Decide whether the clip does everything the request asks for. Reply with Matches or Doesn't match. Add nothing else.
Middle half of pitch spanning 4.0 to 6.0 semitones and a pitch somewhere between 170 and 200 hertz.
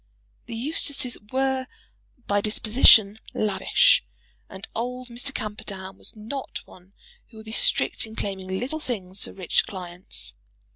Doesn't match